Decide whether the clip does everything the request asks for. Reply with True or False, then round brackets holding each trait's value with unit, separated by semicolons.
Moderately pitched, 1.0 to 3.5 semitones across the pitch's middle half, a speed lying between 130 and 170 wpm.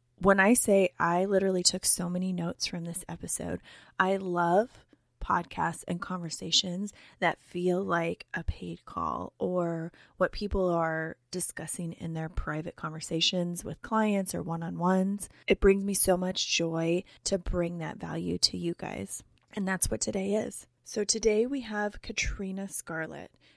True (180 Hz; 2.6 semitones; 160 wpm)